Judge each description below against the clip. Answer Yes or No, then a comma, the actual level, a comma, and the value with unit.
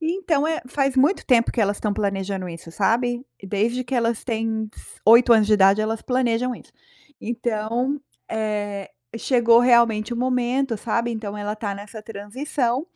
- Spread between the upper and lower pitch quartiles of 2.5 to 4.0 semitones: Yes, average, 3.0 semitones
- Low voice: No, high, 230 Hz